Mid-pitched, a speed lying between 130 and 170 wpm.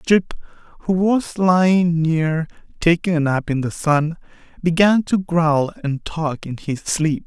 Yes: medium, 165 Hz; average, 155 wpm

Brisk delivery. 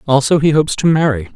Yes: fast, 220 wpm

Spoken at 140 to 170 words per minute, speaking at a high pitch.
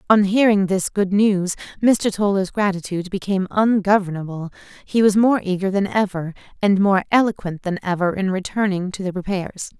Yes: average, 160 wpm; high, 195 Hz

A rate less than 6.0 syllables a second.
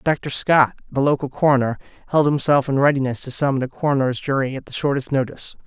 No: 6.4 syllables/s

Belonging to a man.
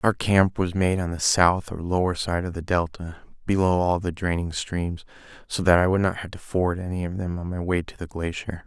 Yes: male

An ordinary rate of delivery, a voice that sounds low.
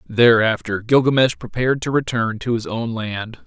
Yes: average, 155 wpm; low, 120 Hz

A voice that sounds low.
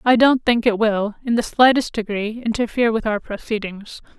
No: high, 225 Hz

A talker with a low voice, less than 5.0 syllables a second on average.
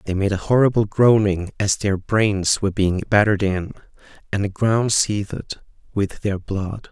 Yes: low, 100 Hz; 4.6 syllables/s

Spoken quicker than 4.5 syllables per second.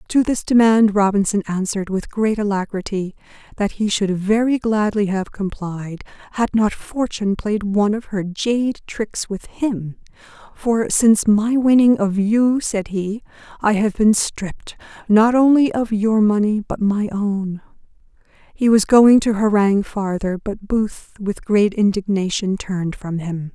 No: 4.3 syllables/s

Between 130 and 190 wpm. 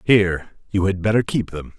No: average, 200 wpm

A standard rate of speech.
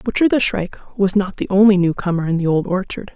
No: fast, 230 wpm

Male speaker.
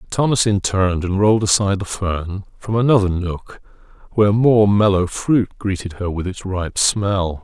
Yes: male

